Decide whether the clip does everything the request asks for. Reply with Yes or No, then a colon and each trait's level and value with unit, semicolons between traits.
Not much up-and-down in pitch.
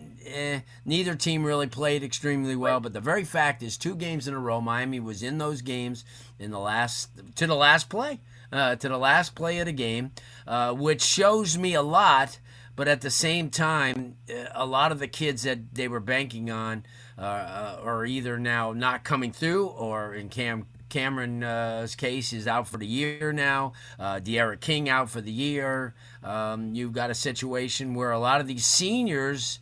No: average, 3.5 semitones